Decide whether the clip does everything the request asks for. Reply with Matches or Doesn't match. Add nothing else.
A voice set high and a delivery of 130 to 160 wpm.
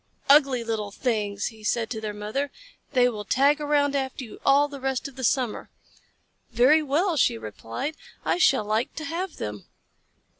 Doesn't match